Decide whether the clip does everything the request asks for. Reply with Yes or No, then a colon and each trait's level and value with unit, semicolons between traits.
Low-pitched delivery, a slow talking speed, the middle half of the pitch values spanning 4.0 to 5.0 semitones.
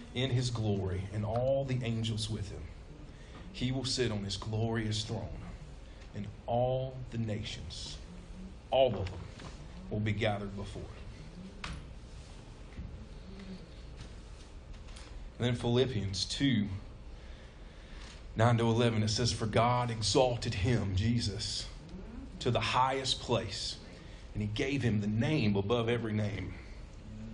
Yes: low, 105 Hz; slow, 120 wpm; average, 4.3 semitones